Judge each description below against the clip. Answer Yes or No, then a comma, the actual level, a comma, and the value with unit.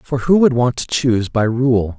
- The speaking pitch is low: Yes, low, 125 Hz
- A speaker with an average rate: No, fast, 240 wpm